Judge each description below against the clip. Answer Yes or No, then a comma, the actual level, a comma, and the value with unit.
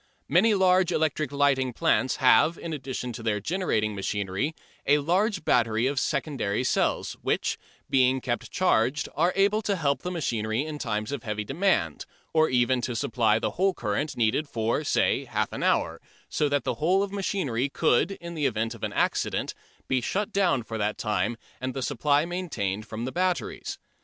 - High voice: No, low, 135 Hz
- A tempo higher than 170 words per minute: Yes, average, 180 wpm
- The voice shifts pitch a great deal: Yes, wide, 6.7 semitones